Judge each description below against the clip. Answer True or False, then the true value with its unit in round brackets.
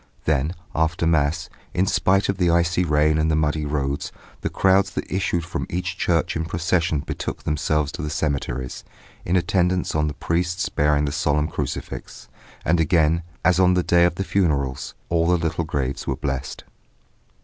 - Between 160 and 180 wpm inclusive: True (175 wpm)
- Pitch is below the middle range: True (80 Hz)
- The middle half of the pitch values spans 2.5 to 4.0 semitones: True (2.9 semitones)